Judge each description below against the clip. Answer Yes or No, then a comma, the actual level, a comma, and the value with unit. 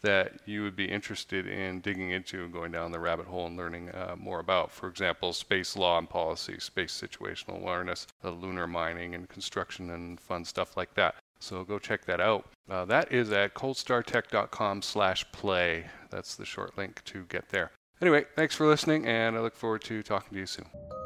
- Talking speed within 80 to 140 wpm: No, average, 195 wpm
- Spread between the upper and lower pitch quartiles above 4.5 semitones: No, average, 3.7 semitones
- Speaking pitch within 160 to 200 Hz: No, very low, 95 Hz